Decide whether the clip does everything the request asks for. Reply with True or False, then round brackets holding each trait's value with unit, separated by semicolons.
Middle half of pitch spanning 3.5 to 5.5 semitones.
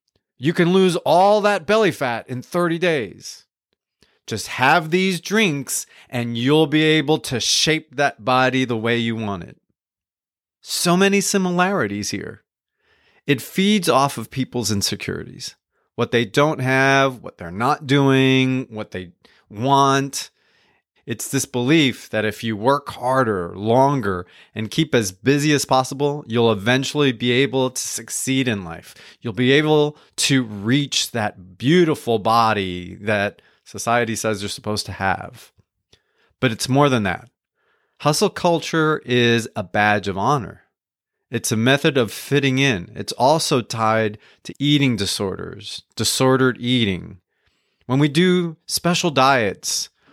True (4.9 semitones)